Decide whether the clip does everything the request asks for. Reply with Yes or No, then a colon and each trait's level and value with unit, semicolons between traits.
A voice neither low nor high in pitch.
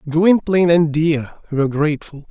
Yes: medium, 160 Hz